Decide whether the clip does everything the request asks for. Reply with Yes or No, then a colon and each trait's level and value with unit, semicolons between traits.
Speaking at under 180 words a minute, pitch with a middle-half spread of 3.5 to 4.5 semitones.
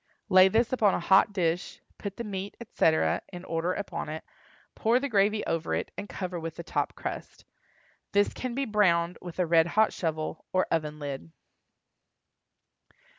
Yes: average, 170 wpm; average, 4.0 semitones